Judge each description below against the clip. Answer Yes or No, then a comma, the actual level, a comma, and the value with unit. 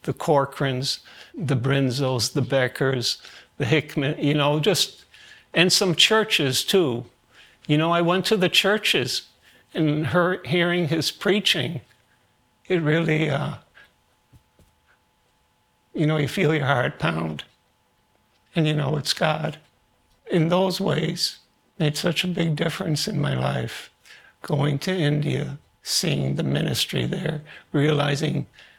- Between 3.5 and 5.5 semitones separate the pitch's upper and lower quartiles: Yes, average, 4.2 semitones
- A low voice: No, medium, 150 Hz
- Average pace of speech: No, slow, 125 wpm